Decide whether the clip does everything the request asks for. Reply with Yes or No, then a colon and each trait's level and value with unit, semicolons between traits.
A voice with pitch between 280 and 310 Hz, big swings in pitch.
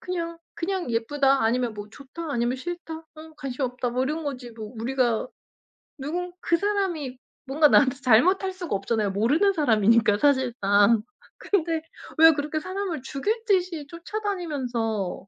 Yes: very high, 285 Hz; wide, 6.1 semitones